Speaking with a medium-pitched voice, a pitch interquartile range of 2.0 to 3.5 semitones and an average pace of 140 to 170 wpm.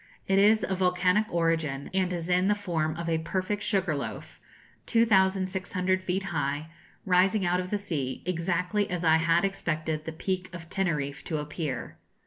Yes: medium, 180 Hz; average, 2.9 semitones; average, 165 wpm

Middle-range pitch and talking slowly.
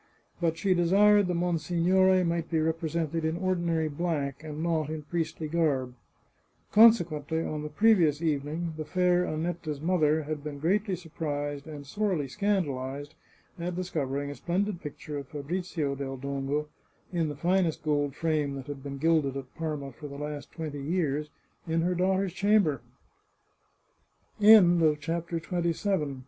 Yes: medium, 155 Hz; slow, 130 wpm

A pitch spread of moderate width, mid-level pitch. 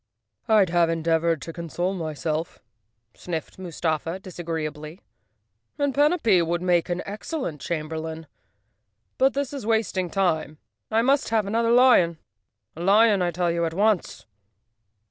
Yes: average, 4.9 semitones; medium, 175 Hz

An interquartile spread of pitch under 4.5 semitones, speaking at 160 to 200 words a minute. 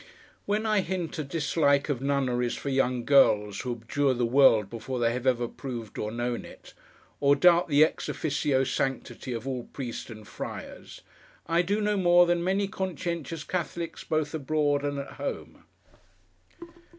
No: average, 5.3 semitones; average, 165 wpm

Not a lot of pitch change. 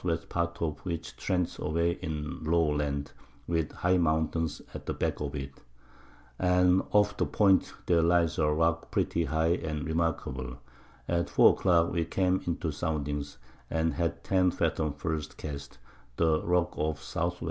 Yes: narrow, 2.1 semitones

